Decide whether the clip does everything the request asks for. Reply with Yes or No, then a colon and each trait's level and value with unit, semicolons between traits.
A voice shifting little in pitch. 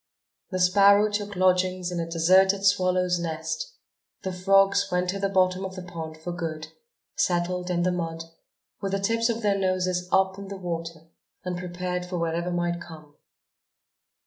Yes: narrow, 2.0 semitones